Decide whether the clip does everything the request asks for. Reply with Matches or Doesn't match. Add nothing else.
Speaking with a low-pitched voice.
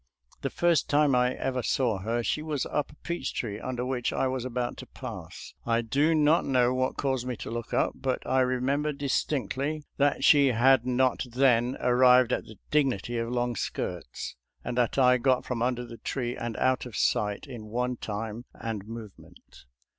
Matches